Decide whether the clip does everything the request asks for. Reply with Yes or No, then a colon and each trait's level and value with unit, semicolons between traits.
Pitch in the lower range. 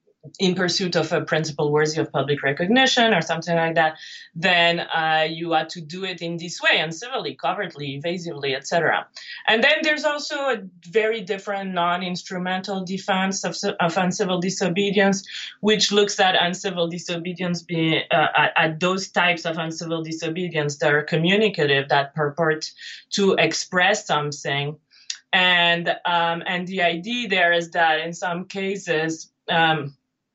No: medium, 175 Hz